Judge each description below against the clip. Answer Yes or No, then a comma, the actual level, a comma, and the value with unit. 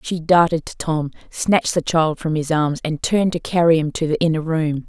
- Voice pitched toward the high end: No, medium, 160 Hz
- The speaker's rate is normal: No, fast, 235 wpm